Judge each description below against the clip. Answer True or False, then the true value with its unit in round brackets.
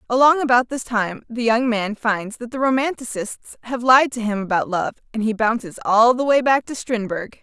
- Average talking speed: False (210 wpm)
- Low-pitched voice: False (235 Hz)